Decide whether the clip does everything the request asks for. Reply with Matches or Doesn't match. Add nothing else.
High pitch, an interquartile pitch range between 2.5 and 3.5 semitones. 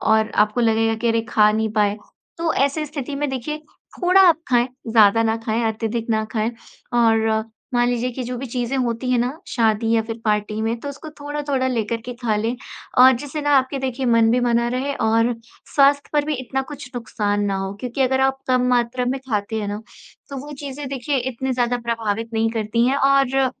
Matches